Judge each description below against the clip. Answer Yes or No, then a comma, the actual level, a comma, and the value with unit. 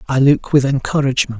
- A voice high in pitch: No, low, 135 Hz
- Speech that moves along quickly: No, average, 170 wpm